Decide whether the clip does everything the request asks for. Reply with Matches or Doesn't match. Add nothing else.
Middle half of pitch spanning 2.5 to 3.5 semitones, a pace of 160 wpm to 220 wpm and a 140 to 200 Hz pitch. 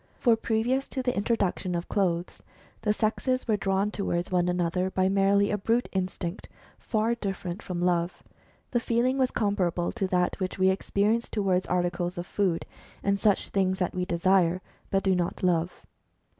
Matches